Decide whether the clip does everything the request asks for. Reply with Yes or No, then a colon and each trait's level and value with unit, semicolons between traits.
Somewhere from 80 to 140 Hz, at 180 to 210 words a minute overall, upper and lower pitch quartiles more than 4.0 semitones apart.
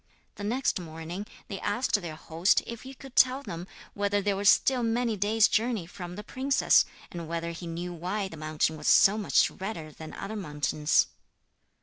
No: high, 195 Hz; average, 185 wpm; average, 4.8 semitones